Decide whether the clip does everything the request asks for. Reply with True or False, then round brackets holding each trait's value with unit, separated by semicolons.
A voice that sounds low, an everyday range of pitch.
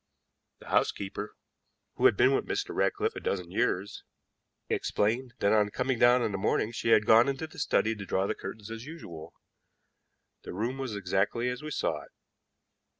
True (115 Hz; 4.5 semitones)